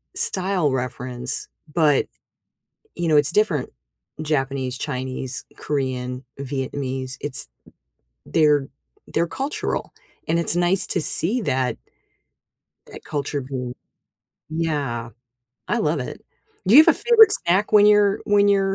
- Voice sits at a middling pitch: Yes, medium, 150 Hz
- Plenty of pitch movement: Yes, wide, 6.4 semitones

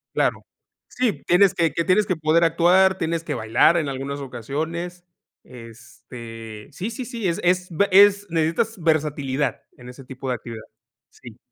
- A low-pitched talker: No, medium, 160 Hz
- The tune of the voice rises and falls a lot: Yes, wide, 5.7 semitones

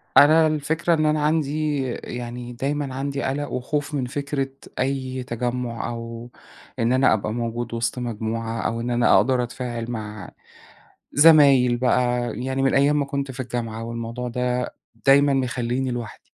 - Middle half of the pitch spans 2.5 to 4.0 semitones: Yes, average, 2.8 semitones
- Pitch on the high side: No, low, 125 Hz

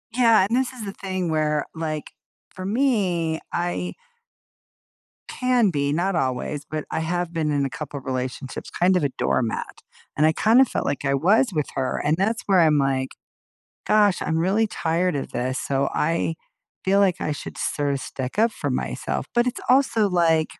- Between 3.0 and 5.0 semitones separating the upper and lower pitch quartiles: No, wide, 5.6 semitones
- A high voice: No, medium, 165 Hz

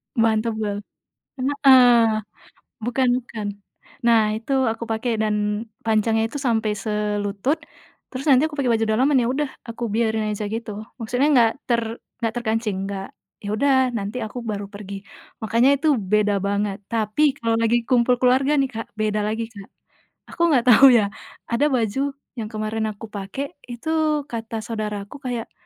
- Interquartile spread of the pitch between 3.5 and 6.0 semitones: No, average, 3.0 semitones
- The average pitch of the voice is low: No, high, 225 Hz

